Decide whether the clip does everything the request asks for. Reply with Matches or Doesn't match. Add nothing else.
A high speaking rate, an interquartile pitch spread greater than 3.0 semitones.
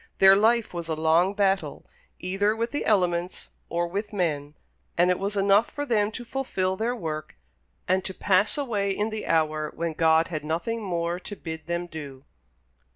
Doesn't match